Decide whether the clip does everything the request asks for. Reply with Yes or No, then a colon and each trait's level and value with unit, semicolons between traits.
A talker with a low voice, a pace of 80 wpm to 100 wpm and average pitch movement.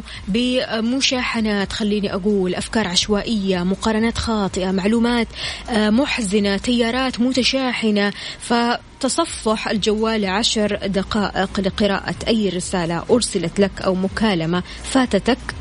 No: high, 215 Hz; average, 90 wpm; average, 3.1 semitones